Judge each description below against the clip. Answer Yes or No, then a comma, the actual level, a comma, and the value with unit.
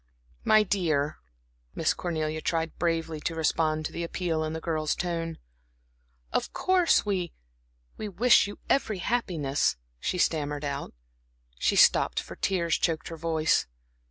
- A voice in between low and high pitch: Yes, medium, 165 Hz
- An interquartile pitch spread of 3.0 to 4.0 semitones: No, narrow, 2.5 semitones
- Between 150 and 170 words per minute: No, average, 140 wpm